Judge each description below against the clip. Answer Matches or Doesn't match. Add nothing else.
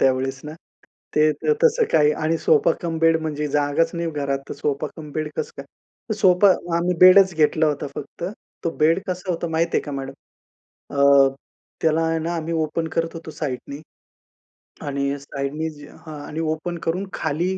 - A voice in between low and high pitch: Matches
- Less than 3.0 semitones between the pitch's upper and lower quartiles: Matches